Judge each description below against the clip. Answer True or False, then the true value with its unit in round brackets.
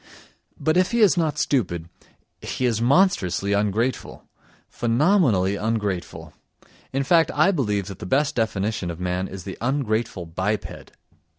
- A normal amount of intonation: False (6.6 semitones)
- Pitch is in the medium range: False (110 Hz)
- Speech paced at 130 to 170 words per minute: True (135 wpm)